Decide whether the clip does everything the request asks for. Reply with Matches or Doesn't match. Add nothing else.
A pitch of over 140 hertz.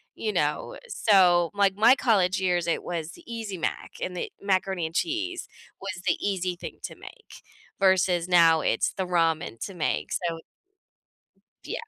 Matches